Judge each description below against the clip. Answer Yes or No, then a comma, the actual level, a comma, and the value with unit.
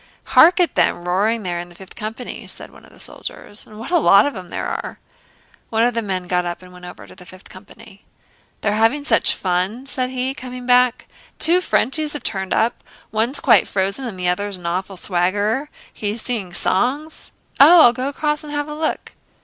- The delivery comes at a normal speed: No, fast, 210 wpm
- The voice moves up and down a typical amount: No, wide, 6.1 semitones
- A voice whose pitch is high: Yes, high, 220 Hz